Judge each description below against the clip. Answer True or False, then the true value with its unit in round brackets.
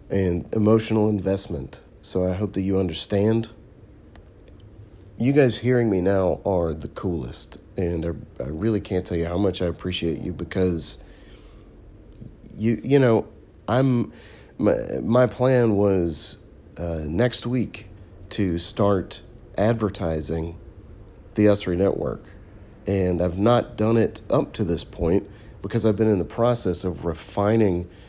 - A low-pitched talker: True (100 Hz)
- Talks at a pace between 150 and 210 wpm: False (140 wpm)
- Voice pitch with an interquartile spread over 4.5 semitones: False (3.8 semitones)